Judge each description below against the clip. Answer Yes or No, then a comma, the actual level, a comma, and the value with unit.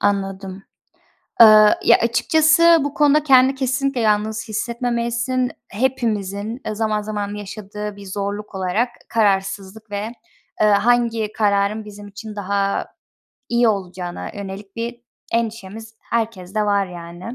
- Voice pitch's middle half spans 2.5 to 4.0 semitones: Yes, average, 2.8 semitones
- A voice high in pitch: Yes, high, 215 Hz